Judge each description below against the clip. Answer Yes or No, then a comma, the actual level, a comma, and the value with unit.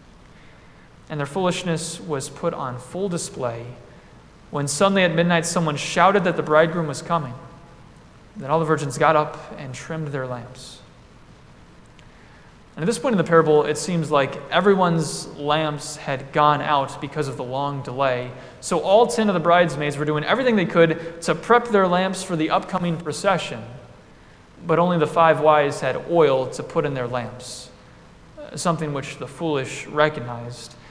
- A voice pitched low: No, medium, 155 Hz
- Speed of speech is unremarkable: Yes, average, 165 wpm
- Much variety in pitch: No, average, 3.6 semitones